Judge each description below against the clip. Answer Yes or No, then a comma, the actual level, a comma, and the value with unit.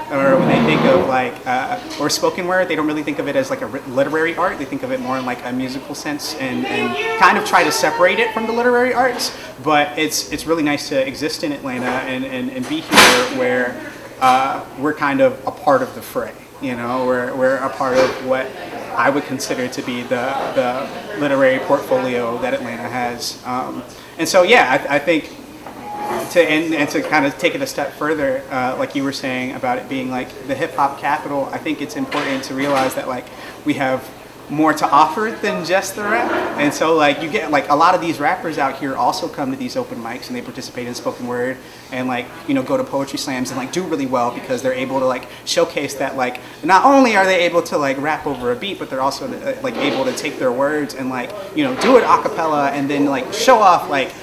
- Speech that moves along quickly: Yes, fast, 240 wpm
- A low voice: No, medium, 150 Hz